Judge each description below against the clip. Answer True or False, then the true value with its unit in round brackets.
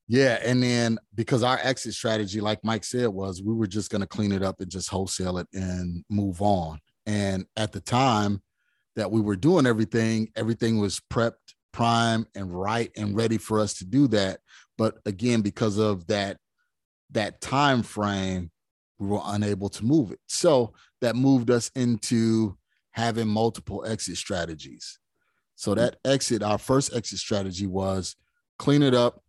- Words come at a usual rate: True (170 wpm)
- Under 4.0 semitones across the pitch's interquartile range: True (2.9 semitones)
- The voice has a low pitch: True (110 Hz)